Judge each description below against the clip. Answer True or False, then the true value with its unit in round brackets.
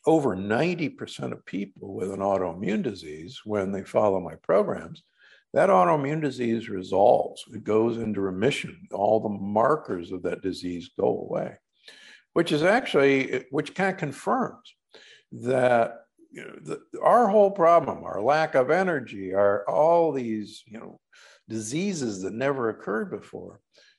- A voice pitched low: True (115 Hz)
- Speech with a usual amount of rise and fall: False (7.0 semitones)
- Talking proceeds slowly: False (145 wpm)